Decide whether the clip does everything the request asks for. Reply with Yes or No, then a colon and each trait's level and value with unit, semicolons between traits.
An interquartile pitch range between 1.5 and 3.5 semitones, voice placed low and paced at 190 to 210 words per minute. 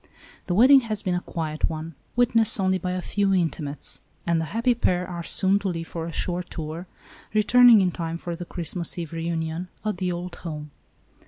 No: average, 3.1 semitones; medium, 175 Hz; average, 200 wpm